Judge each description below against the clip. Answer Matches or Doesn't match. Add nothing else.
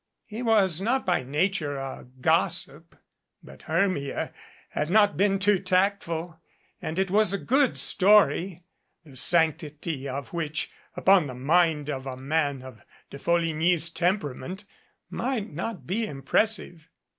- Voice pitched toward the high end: Doesn't match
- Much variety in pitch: Doesn't match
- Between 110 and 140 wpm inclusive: Matches